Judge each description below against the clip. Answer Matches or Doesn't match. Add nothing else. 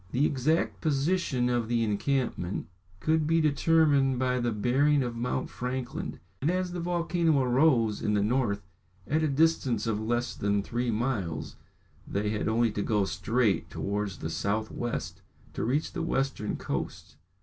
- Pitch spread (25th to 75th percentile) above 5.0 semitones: Matches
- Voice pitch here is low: Matches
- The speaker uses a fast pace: Doesn't match